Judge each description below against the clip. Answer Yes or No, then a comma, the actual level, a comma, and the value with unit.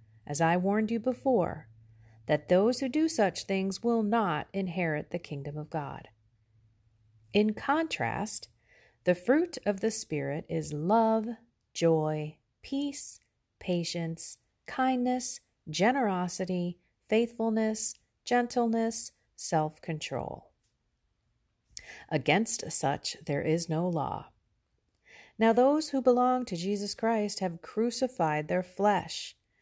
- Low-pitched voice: No, high, 195 Hz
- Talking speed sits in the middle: No, slow, 105 wpm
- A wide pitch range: Yes, wide, 6.6 semitones